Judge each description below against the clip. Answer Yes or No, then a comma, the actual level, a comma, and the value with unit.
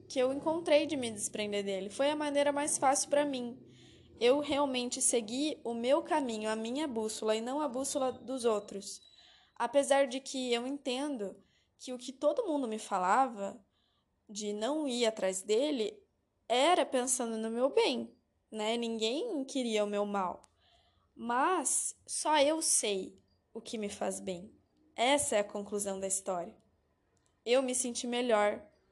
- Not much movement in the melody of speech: No, average, 4.8 semitones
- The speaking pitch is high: Yes, high, 245 Hz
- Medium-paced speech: Yes, average, 160 wpm